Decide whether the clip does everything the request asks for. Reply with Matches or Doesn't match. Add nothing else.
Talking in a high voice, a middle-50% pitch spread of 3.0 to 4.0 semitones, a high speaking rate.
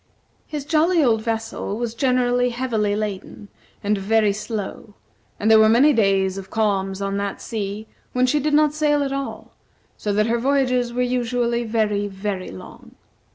Doesn't match